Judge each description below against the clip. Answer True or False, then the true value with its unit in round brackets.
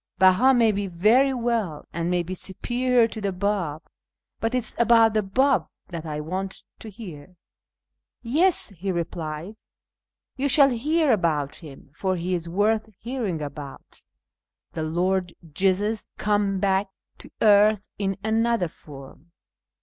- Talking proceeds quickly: False (150 wpm)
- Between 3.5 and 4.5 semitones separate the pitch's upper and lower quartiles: False (5.0 semitones)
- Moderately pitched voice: False (195 Hz)